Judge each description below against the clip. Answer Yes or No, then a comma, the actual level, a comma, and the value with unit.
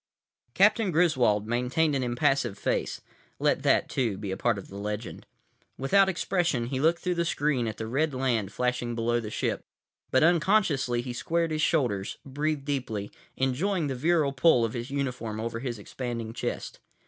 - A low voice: Yes, low, 130 Hz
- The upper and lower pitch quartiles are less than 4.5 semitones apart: No, average, 5.0 semitones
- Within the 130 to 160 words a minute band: No, average, 175 wpm